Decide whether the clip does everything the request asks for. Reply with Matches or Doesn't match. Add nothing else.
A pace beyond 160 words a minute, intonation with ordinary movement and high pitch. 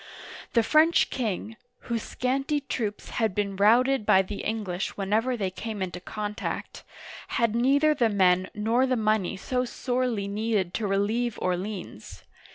Doesn't match